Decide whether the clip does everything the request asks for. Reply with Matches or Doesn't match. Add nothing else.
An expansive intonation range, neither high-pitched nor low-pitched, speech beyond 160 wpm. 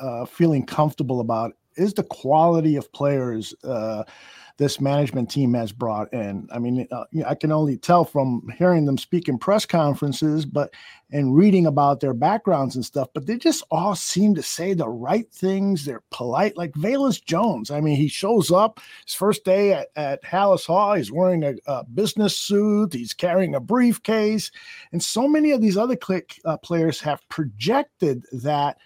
Matches